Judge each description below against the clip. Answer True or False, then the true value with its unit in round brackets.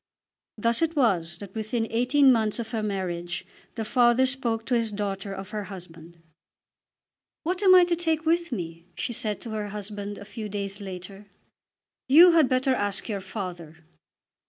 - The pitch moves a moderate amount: True (4.6 semitones)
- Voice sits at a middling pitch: False (215 Hz)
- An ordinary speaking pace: True (170 wpm)